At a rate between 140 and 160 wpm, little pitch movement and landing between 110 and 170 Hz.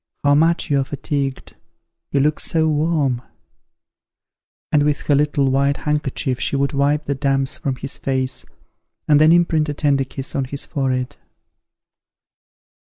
Yes: average, 150 wpm; narrow, 1.7 semitones; medium, 140 Hz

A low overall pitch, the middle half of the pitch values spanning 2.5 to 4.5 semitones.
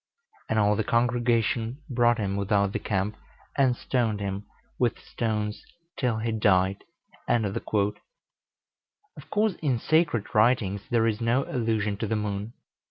Yes: low, 110 Hz; average, 2.8 semitones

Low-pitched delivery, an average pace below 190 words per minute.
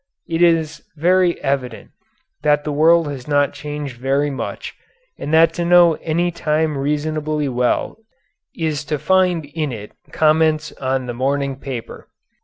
No: medium, 150 Hz; average, 145 wpm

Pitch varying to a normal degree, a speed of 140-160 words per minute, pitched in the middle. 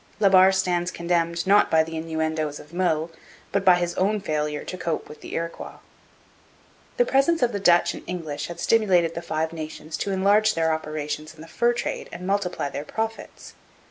No: average, 3.5 semitones; average, 190 wpm; medium, 170 Hz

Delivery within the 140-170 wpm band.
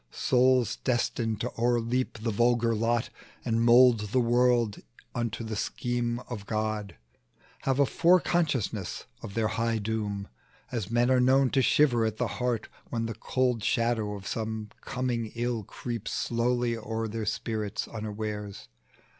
Yes: average, 145 wpm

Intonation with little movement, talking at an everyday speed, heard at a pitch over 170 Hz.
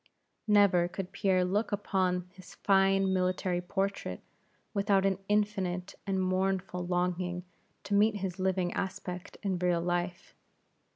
No: narrow, 1.5 semitones; slow, 125 wpm; medium, 185 Hz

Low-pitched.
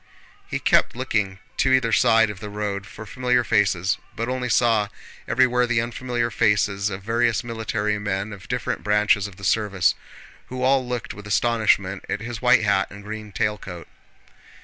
Yes: low, 110 Hz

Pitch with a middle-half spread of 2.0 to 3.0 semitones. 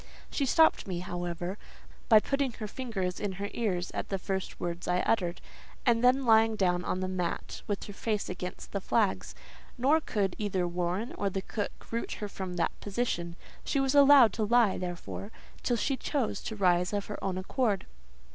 No: average, 4.4 semitones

